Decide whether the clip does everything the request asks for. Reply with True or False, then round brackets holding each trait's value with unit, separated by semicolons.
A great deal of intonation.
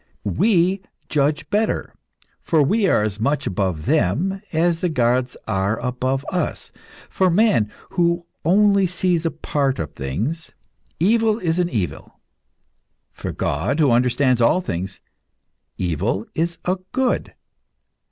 True (7.7 semitones)